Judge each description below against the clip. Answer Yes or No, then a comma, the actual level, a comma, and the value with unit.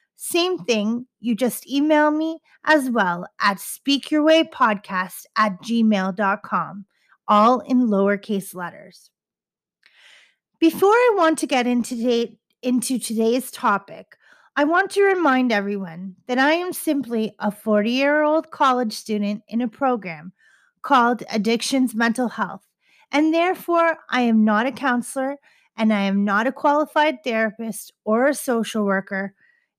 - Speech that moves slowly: Yes, slow, 130 wpm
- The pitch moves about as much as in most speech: No, wide, 6.1 semitones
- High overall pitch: Yes, high, 240 Hz